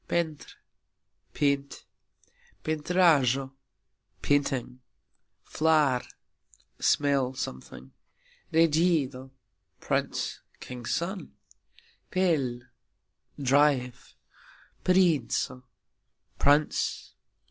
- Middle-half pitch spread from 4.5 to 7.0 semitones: No, average, 3.8 semitones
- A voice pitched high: No, medium, 145 Hz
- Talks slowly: Yes, slow, 50 wpm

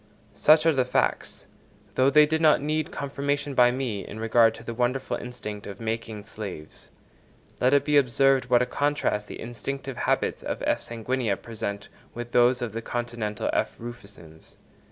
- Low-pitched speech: Yes, low, 120 Hz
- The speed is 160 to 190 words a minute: Yes, average, 170 wpm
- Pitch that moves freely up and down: No, average, 3.6 semitones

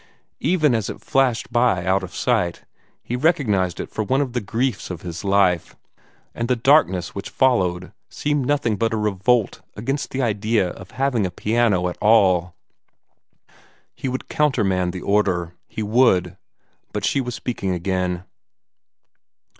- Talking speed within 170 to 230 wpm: No, average, 155 wpm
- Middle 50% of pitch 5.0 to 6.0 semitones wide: Yes, average, 5.3 semitones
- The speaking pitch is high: No, low, 105 Hz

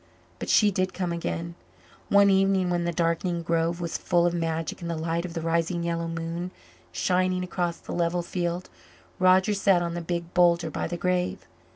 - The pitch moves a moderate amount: No, narrow, 1.4 semitones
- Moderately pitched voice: Yes, medium, 175 Hz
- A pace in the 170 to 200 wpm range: Yes, average, 190 wpm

